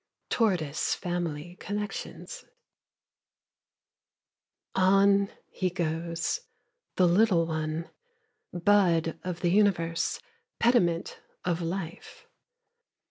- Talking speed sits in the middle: No, slow, 75 wpm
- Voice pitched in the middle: Yes, medium, 175 Hz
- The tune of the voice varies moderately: Yes, average, 3.0 semitones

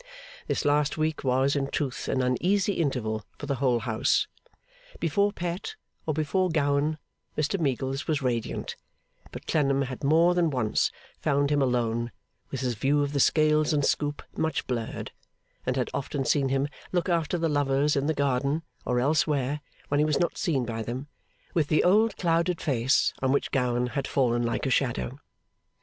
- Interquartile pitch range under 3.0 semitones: No, average, 3.3 semitones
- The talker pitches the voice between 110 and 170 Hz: Yes, medium, 140 Hz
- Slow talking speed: No, average, 175 wpm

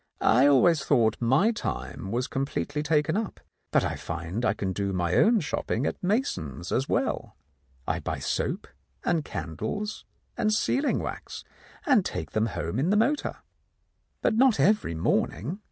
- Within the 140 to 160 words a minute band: Yes, average, 155 wpm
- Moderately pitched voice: Yes, medium, 145 Hz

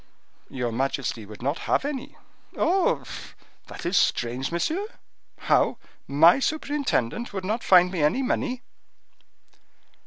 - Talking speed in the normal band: No, slow, 120 wpm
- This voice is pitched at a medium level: Yes, medium, 180 Hz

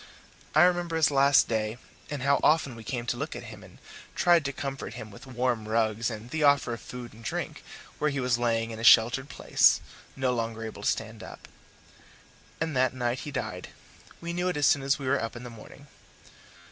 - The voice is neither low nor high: No, low, 125 Hz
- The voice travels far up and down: No, average, 3.7 semitones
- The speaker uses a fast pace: Yes, fast, 215 wpm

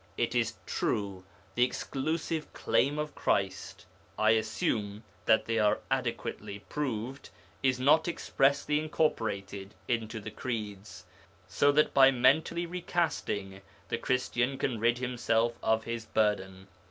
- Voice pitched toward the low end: Yes, low, 120 Hz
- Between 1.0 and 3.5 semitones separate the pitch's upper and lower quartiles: No, average, 4.6 semitones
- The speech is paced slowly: Yes, slow, 125 wpm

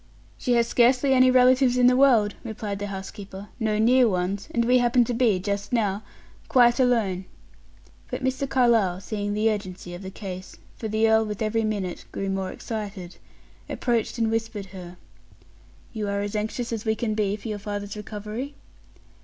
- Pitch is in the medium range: No, high, 215 Hz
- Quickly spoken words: No, average, 180 wpm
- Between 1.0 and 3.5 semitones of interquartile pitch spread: Yes, average, 3.0 semitones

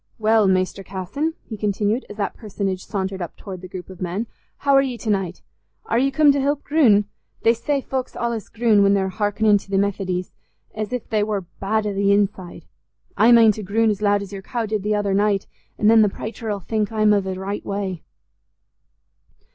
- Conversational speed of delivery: No, fast, 210 wpm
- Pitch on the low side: No, high, 205 Hz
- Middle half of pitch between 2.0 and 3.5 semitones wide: Yes, narrow, 2.5 semitones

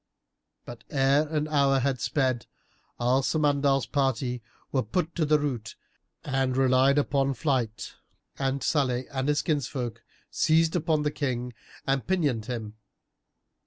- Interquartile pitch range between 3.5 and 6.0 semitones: No, average, 2.8 semitones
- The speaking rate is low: Yes, slow, 130 wpm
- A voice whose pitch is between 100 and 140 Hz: Yes, low, 135 Hz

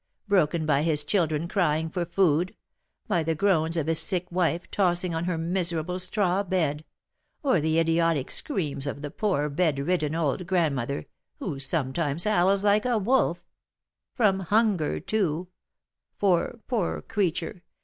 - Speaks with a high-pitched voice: No, medium, 170 Hz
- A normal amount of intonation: Yes, average, 3.5 semitones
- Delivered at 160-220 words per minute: No, average, 140 wpm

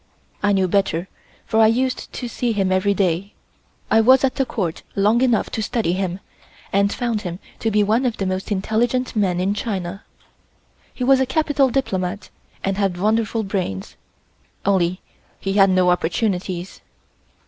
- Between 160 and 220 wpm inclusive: Yes, average, 165 wpm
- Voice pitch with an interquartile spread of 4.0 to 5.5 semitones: No, average, 3.5 semitones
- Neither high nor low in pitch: No, high, 200 Hz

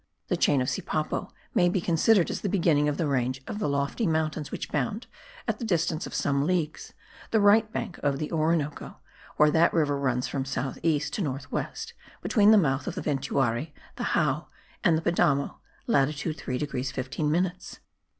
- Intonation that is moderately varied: Yes, average, 3.9 semitones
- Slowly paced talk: No, average, 185 wpm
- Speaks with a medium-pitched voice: Yes, medium, 150 Hz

